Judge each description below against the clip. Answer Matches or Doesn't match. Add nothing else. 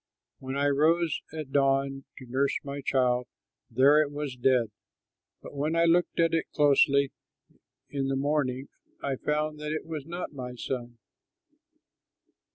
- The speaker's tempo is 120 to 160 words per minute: Matches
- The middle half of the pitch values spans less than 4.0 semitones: Matches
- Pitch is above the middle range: Doesn't match